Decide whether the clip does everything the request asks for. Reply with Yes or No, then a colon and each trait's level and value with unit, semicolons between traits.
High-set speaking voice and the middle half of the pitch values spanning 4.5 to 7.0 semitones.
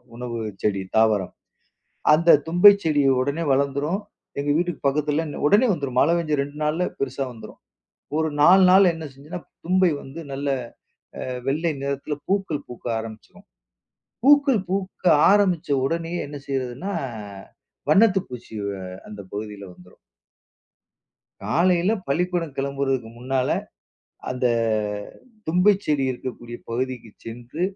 No: medium, 145 Hz; wide, 5.5 semitones